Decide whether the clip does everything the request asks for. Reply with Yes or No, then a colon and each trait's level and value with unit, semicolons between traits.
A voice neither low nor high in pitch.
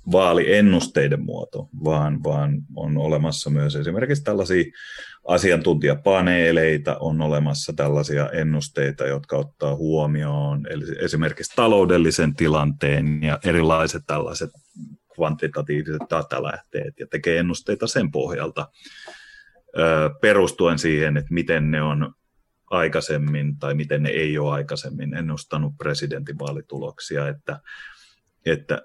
No: very low, 75 Hz